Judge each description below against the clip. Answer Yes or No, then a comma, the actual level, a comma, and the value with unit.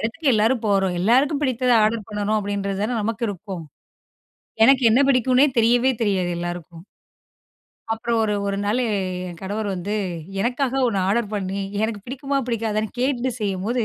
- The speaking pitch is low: No, high, 220 Hz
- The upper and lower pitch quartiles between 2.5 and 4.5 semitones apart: Yes, average, 3.8 semitones